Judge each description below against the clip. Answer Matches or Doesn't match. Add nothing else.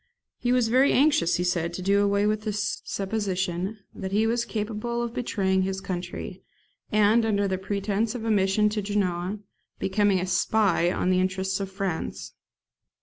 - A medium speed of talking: Matches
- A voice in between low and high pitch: Doesn't match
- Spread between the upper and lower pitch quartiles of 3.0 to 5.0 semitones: Doesn't match